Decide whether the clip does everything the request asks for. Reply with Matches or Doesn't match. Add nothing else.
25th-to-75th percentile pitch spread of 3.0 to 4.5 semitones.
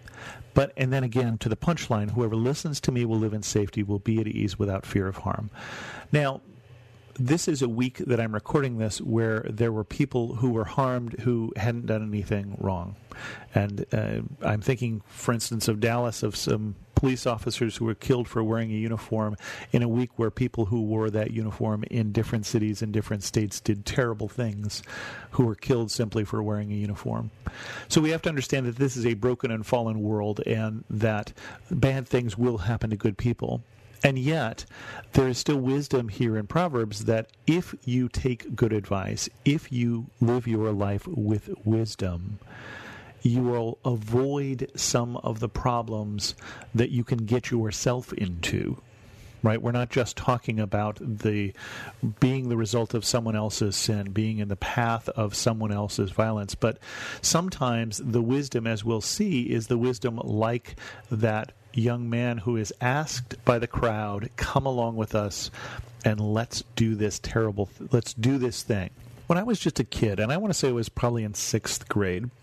Doesn't match